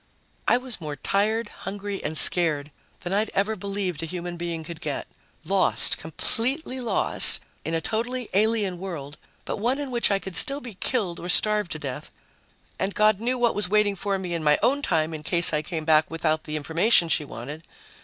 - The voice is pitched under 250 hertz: Yes, high, 190 Hz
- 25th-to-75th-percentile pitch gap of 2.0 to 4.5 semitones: No, average, 5.2 semitones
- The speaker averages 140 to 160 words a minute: No, average, 195 wpm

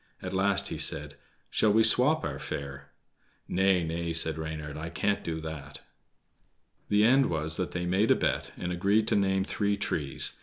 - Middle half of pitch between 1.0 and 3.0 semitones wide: No, average, 4.3 semitones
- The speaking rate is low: No, average, 180 wpm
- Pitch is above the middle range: No, very low, 90 Hz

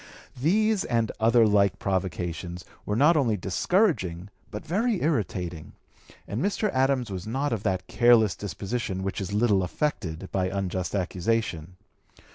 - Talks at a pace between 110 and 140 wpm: Yes, slow, 135 wpm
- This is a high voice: No, low, 105 Hz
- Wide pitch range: Yes, wide, 6.0 semitones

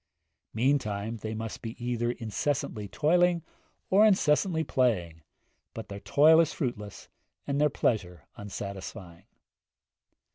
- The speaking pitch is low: Yes, low, 120 Hz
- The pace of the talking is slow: Yes, slow, 110 wpm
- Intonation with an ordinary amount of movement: No, wide, 6.4 semitones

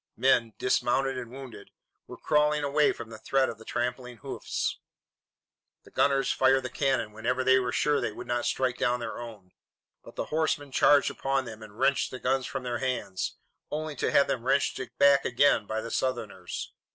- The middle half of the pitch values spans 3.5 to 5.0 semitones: No, narrow, 2.6 semitones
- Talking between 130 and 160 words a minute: No, average, 190 wpm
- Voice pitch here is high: No, low, 130 Hz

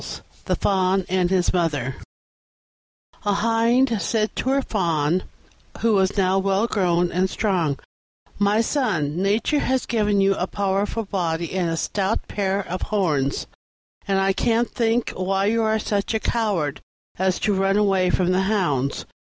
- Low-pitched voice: No, high, 195 Hz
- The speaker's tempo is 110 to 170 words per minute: Yes, average, 155 wpm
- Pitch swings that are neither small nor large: Yes, average, 3.0 semitones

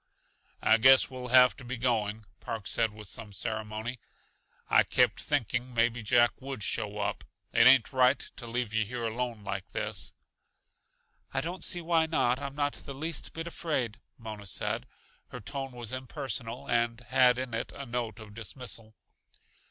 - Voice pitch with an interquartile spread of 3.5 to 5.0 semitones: No, average, 2.8 semitones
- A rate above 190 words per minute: No, average, 170 wpm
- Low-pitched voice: Yes, low, 120 Hz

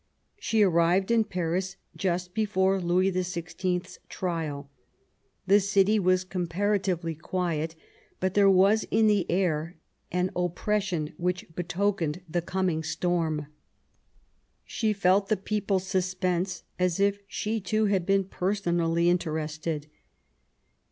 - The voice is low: No, medium, 185 Hz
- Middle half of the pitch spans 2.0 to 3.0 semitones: Yes, narrow, 2.4 semitones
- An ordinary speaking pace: No, slow, 115 wpm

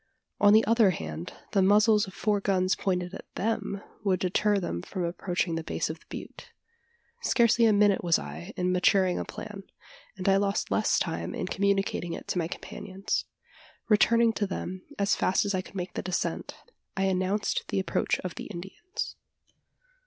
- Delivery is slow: No, average, 180 wpm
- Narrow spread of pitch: Yes, narrow, 2.2 semitones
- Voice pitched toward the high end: Yes, high, 195 Hz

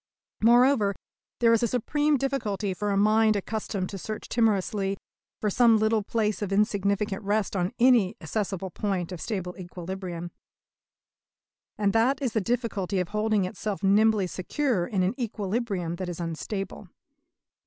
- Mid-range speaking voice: No, high, 205 Hz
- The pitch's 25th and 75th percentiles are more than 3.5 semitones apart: No, average, 2.9 semitones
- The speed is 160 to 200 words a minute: No, average, 145 wpm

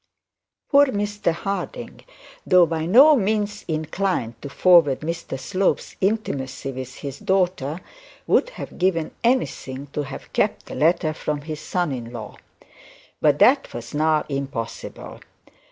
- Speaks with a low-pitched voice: No, medium, 160 Hz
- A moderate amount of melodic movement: No, wide, 6.1 semitones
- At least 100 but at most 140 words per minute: Yes, slow, 135 wpm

